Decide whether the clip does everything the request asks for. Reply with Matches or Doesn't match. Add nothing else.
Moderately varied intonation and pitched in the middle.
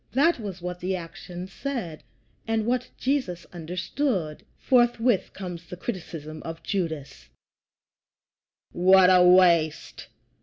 Matches